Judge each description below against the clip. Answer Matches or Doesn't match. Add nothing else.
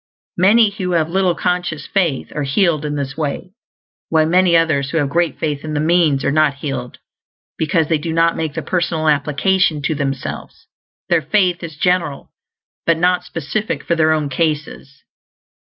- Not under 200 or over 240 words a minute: Doesn't match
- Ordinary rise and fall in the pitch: Matches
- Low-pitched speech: Doesn't match